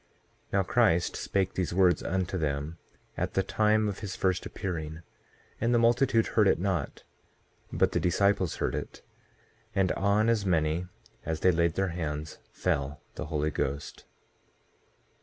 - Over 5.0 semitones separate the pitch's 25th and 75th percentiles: No, average, 4.0 semitones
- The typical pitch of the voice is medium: No, very low, 90 Hz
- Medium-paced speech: Yes, average, 155 wpm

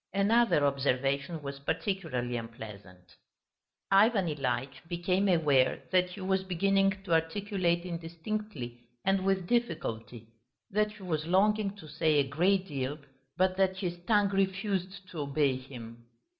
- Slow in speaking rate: Yes, slow, 130 wpm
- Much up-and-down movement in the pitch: Yes, wide, 5.9 semitones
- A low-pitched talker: No, medium, 175 Hz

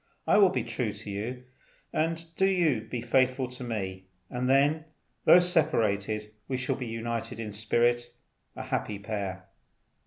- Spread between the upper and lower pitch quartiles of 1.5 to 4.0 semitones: Yes, average, 3.6 semitones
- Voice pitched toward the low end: Yes, low, 120 Hz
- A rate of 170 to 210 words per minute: No, average, 150 wpm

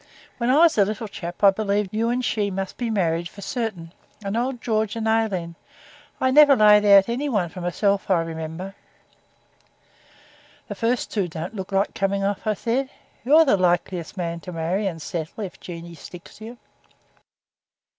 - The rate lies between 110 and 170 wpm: No, average, 180 wpm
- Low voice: No, high, 200 Hz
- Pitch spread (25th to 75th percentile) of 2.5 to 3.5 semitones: No, average, 4.3 semitones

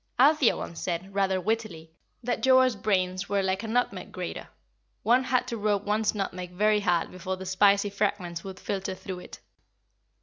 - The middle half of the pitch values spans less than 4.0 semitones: Yes, average, 2.9 semitones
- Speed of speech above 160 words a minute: Yes, average, 170 wpm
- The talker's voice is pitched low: No, high, 200 Hz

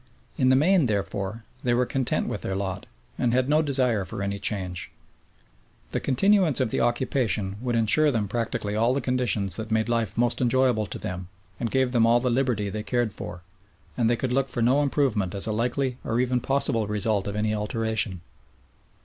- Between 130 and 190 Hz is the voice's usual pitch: No, low, 115 Hz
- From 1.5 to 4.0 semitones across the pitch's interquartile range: Yes, average, 3.4 semitones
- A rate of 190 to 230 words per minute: Yes, average, 195 wpm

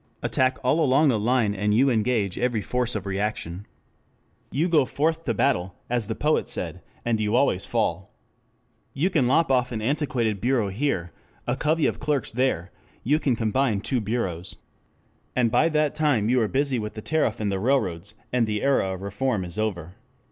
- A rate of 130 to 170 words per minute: No, average, 185 wpm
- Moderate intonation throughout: Yes, average, 4.7 semitones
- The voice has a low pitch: Yes, low, 120 Hz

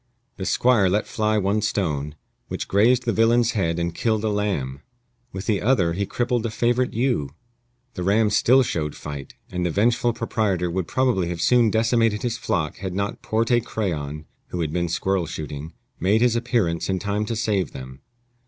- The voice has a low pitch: Yes, low, 100 Hz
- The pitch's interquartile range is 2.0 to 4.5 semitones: No, average, 5.1 semitones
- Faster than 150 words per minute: Yes, average, 180 wpm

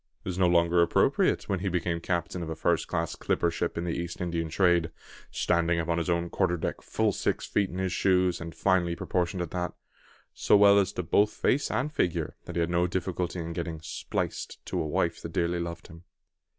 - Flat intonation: Yes, narrow, 1.5 semitones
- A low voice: Yes, very low, 85 Hz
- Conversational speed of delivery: No, fast, 220 wpm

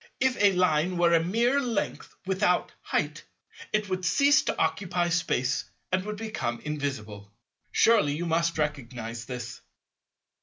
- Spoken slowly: Yes, slow, 130 wpm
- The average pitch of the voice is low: No, medium, 170 Hz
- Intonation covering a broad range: Yes, wide, 6.2 semitones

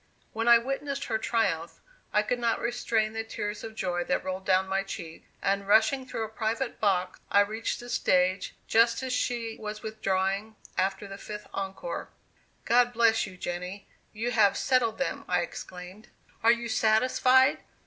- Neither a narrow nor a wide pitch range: Yes, average, 3.4 semitones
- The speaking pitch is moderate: No, high, 220 Hz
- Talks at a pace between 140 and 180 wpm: Yes, average, 170 wpm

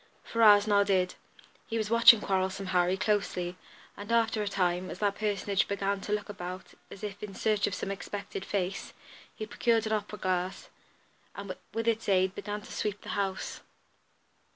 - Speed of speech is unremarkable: Yes, average, 170 wpm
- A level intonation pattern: Yes, narrow, 1.9 semitones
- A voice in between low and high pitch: No, high, 200 Hz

